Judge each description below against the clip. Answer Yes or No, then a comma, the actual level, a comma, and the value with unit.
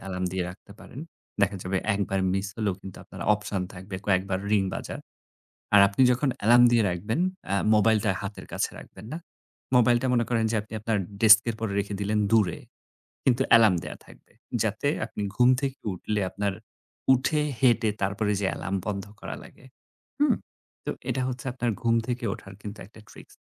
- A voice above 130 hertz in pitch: No, low, 105 Hz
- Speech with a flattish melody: No, average, 3.3 semitones